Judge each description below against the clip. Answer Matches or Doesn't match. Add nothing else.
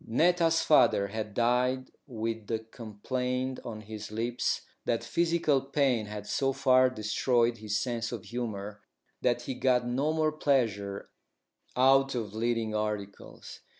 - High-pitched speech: Doesn't match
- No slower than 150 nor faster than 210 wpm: Doesn't match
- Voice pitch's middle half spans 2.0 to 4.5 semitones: Matches